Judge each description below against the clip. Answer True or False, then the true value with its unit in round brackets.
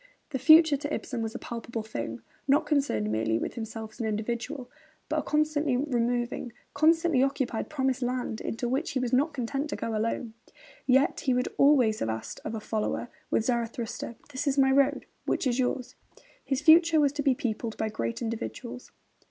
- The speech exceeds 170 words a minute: True (185 wpm)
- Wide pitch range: False (4.0 semitones)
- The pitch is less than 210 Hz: False (250 Hz)